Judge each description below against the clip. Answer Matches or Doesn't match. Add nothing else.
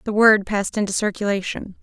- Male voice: Doesn't match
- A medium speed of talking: Matches